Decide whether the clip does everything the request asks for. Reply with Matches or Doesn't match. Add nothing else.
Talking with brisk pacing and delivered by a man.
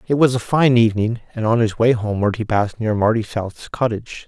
Matches